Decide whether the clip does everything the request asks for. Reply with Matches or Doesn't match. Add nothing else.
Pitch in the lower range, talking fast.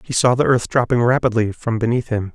Matches